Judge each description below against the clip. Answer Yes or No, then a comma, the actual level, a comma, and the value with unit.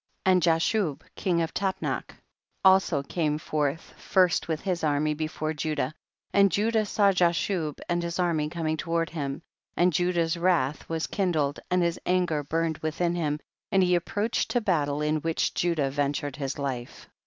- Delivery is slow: No, average, 180 wpm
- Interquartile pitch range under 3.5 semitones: Yes, average, 3.1 semitones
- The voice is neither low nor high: Yes, medium, 165 Hz